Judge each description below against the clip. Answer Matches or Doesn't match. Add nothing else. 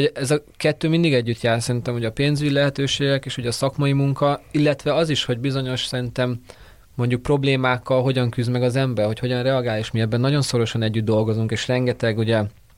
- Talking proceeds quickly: Matches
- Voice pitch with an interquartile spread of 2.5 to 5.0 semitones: Matches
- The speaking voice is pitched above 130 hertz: Doesn't match